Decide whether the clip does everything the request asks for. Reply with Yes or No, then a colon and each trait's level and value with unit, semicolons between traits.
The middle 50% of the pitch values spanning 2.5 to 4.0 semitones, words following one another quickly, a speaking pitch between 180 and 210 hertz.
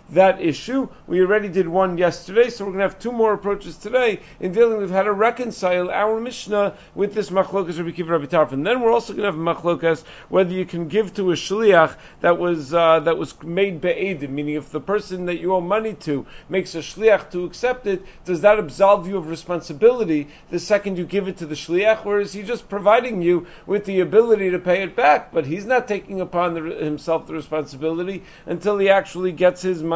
Yes: average, 3.4 semitones; fast, 220 wpm; medium, 185 Hz